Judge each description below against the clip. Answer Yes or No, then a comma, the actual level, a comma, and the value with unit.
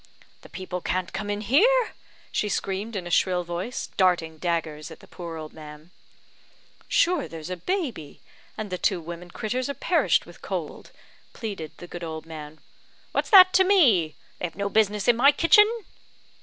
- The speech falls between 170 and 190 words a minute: Yes, average, 175 wpm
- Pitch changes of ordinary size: No, wide, 6.4 semitones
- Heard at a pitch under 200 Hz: Yes, medium, 185 Hz